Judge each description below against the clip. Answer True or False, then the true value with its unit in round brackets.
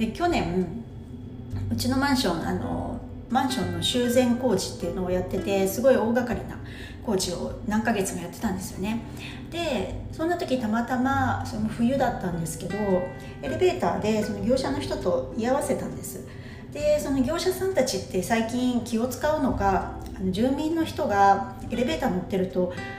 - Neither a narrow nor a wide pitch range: False (6.3 semitones)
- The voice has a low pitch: False (225 Hz)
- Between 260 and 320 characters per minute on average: True (315 characters per minute)